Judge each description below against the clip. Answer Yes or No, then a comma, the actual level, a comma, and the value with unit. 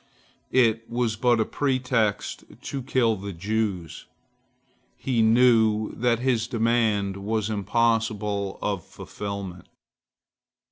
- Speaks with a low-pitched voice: Yes, low, 110 Hz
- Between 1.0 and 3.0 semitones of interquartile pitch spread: Yes, average, 2.7 semitones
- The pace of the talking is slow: Yes, slow, 100 wpm